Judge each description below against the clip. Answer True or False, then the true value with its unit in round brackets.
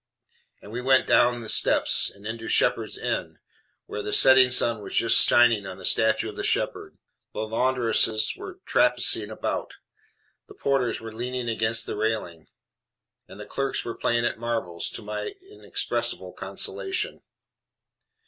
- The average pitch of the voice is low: True (115 Hz)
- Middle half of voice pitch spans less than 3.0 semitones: True (2.4 semitones)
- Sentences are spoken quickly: False (150 wpm)